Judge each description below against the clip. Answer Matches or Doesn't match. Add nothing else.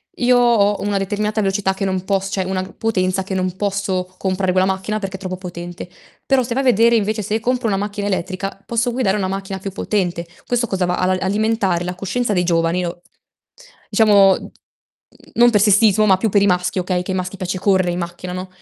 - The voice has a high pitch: Matches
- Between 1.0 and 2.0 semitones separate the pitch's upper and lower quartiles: Doesn't match